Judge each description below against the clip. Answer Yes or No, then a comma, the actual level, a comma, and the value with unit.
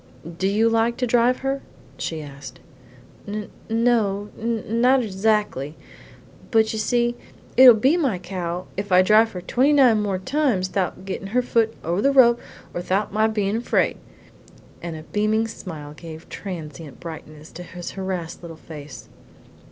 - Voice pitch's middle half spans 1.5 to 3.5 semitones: No, average, 4.8 semitones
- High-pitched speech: Yes, high, 205 Hz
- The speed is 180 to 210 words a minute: No, average, 160 wpm